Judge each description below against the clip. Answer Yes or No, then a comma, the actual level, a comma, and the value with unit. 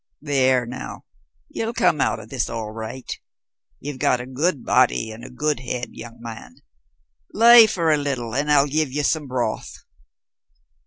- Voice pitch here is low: Yes, low, 130 Hz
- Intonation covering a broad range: No, average, 3.8 semitones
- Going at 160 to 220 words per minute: Yes, average, 165 wpm